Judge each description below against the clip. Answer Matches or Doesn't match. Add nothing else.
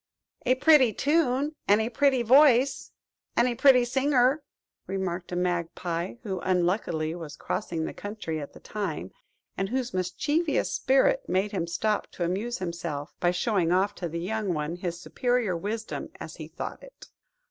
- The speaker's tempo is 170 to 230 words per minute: Doesn't match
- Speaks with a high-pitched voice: Matches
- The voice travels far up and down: Matches